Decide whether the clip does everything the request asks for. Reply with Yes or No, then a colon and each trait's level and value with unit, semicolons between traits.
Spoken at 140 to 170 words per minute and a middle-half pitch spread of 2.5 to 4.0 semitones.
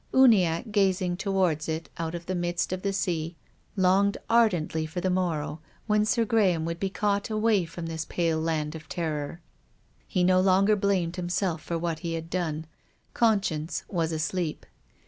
Yes: average, 165 wpm; average, 3.2 semitones